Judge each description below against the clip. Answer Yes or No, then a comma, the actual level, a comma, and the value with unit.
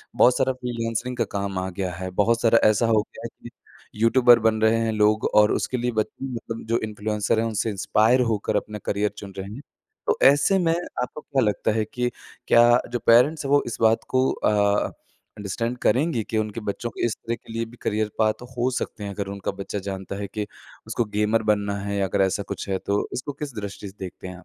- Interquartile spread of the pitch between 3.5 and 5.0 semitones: No, average, 2.9 semitones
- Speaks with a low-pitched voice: Yes, low, 110 Hz